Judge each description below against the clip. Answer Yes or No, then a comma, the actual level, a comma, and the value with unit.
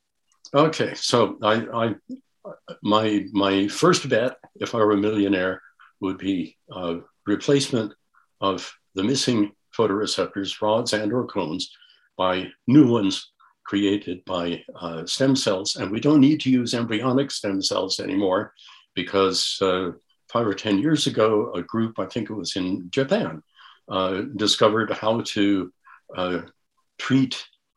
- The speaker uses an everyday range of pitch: Yes, average, 3.3 semitones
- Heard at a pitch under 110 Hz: Yes, low, 100 Hz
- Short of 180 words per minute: Yes, average, 140 wpm